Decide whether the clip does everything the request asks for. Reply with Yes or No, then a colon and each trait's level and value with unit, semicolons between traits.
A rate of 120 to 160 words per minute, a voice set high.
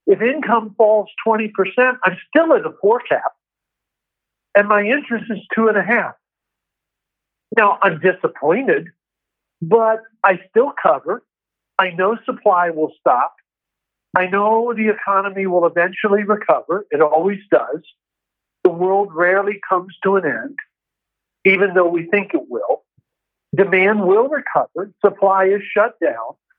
Yes: average, 140 wpm; high, 205 Hz